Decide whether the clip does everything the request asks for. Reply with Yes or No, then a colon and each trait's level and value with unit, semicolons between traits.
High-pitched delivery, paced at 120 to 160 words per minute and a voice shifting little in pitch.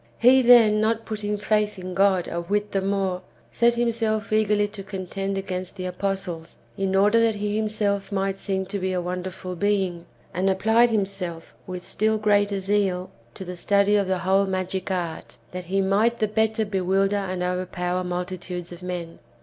No: high, 195 Hz; average, 180 wpm; narrow, 2.3 semitones